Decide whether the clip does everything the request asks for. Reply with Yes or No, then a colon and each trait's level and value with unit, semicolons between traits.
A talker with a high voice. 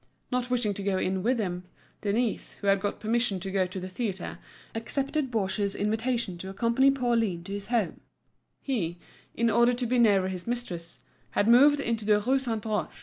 Yes: high, 215 Hz